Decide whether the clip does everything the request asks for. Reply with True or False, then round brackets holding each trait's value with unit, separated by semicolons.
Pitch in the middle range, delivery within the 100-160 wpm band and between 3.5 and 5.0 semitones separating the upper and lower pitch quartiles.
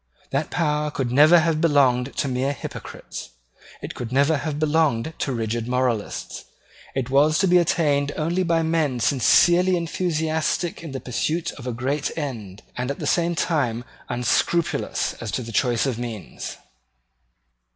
True (145 Hz; 155 wpm; 4.5 semitones)